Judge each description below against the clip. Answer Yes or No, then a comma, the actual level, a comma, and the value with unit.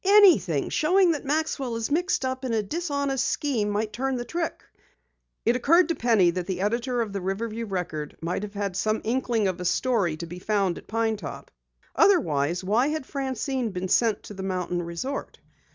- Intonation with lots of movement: Yes, wide, 6.1 semitones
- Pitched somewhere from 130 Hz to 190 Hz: No, high, 225 Hz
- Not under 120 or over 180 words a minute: No, average, 190 wpm